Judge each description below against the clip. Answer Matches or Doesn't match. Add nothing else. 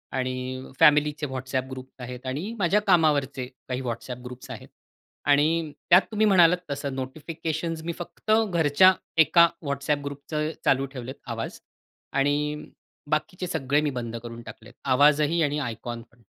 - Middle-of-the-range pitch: Matches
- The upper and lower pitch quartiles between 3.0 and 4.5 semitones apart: Matches